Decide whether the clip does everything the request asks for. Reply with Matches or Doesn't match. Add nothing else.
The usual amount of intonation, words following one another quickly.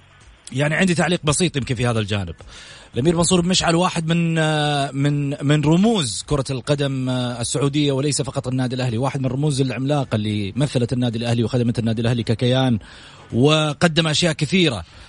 Matches